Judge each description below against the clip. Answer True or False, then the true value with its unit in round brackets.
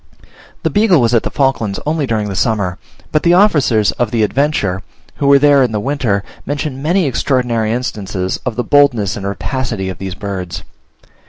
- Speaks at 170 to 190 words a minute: True (180 wpm)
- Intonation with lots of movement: True (5.8 semitones)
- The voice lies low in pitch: True (120 Hz)